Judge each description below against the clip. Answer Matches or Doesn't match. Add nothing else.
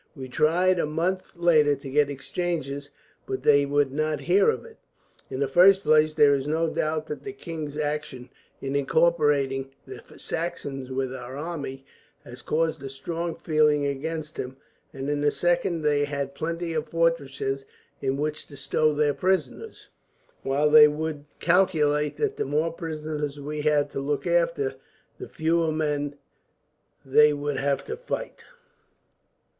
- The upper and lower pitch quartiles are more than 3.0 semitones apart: Doesn't match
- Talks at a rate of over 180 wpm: Doesn't match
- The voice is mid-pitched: Matches